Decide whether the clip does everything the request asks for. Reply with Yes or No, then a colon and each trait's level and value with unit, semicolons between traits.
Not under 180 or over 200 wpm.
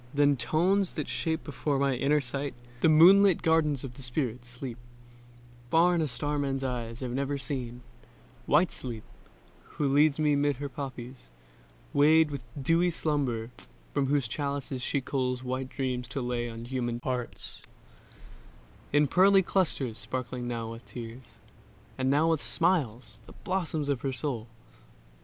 No: average, 150 wpm